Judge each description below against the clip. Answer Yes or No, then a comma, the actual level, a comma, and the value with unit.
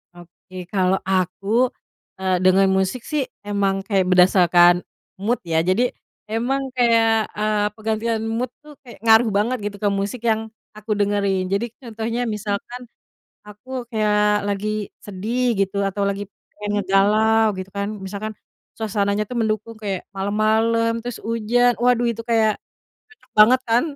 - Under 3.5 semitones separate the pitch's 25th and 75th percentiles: Yes, narrow, 2.6 semitones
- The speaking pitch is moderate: No, high, 210 Hz